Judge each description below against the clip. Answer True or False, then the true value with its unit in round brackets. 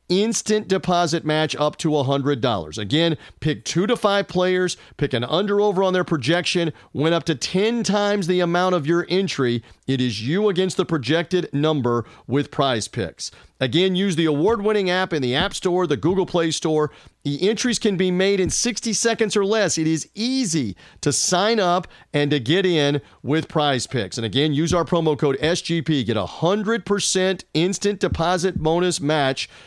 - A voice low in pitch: False (170 Hz)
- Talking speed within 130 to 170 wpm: False (180 wpm)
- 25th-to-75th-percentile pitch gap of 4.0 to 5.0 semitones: True (4.6 semitones)